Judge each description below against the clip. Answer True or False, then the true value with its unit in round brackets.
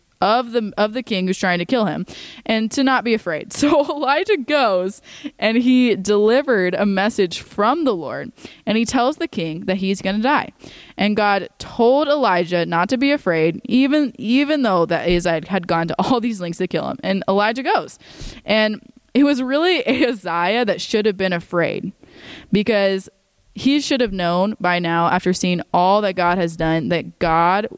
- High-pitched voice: True (210 Hz)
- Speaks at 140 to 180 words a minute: False (190 wpm)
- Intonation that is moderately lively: False (6.0 semitones)